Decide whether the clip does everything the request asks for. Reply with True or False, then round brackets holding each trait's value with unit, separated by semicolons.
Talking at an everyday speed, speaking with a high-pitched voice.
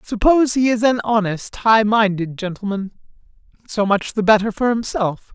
True (145 wpm; 215 Hz)